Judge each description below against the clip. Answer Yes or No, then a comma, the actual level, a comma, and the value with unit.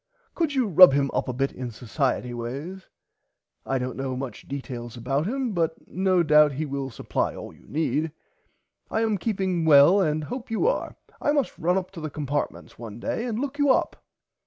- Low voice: No, medium, 155 Hz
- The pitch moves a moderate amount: No, wide, 6.5 semitones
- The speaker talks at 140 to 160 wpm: No, average, 195 wpm